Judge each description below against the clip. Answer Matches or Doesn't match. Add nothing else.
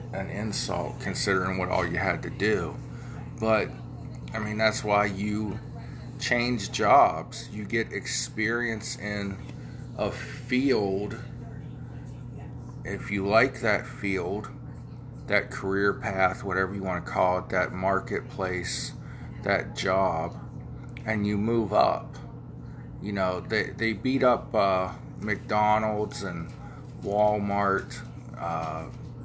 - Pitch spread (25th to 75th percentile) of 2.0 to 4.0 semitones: Matches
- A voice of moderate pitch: Doesn't match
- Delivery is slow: Matches